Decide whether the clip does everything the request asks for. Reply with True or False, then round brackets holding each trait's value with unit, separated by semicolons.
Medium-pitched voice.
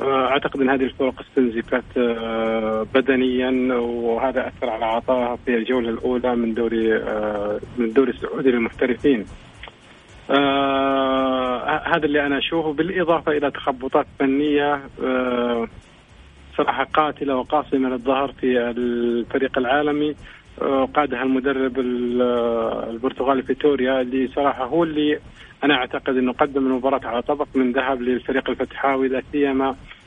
False (130 Hz)